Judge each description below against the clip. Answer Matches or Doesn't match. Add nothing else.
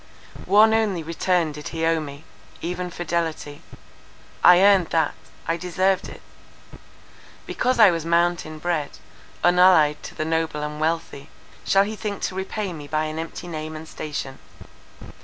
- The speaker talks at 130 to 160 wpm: Matches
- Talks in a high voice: Doesn't match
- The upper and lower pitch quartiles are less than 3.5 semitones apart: Matches